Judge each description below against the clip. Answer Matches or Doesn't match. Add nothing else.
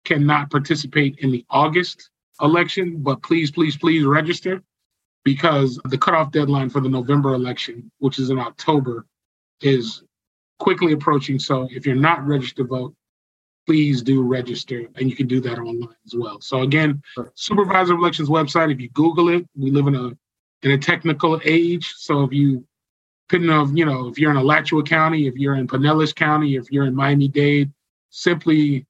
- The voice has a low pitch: Doesn't match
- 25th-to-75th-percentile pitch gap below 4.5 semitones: Matches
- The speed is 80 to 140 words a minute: Doesn't match